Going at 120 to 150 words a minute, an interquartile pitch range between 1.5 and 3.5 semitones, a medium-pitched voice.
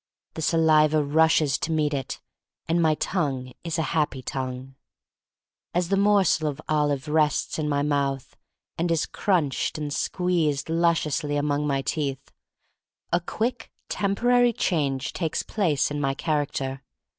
Yes: average, 140 wpm; average, 2.9 semitones; medium, 155 Hz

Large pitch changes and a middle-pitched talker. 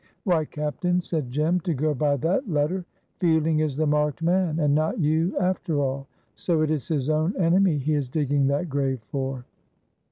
No: average, 3.0 semitones; medium, 155 Hz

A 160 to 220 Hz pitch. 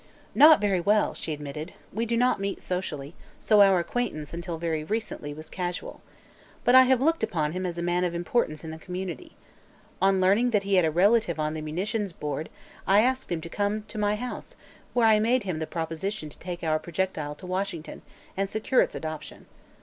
Yes: medium, 185 Hz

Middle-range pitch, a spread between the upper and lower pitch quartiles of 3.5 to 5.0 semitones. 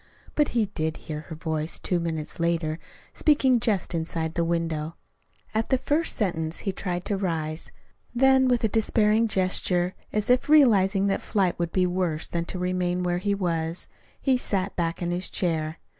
Yes: medium, 180 Hz; average, 4.2 semitones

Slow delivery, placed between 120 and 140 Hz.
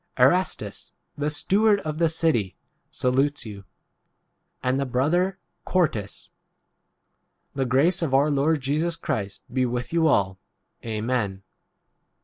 Yes: slow, 130 wpm; low, 135 Hz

